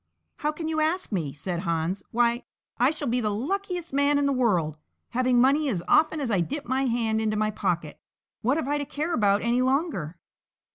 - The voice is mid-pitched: No, high, 245 Hz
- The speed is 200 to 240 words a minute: Yes, fast, 205 wpm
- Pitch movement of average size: No, wide, 6.1 semitones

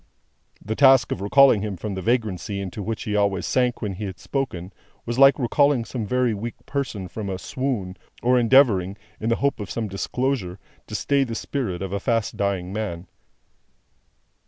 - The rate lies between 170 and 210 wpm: Yes, average, 180 wpm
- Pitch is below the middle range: Yes, low, 110 Hz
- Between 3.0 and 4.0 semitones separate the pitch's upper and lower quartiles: No, average, 4.5 semitones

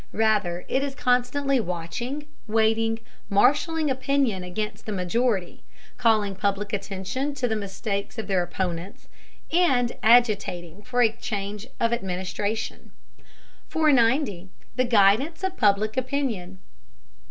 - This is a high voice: Yes, high, 220 Hz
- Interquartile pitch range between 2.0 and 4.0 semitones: No, average, 4.4 semitones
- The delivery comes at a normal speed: No, slow, 115 wpm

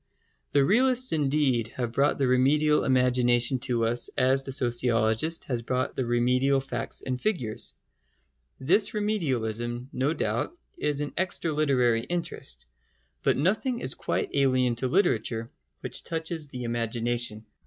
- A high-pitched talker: No, low, 130 Hz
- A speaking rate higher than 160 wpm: No, slow, 135 wpm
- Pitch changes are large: No, average, 4.0 semitones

